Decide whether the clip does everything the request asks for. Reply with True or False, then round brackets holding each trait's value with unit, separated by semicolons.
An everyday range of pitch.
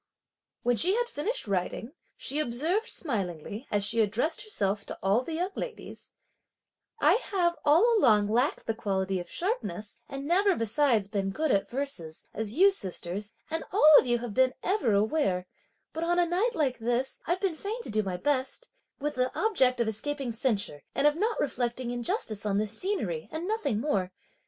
False (8.3 semitones)